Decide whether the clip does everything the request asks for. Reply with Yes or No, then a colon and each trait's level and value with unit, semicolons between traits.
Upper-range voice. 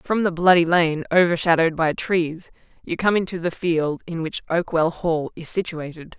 No: medium, 170 Hz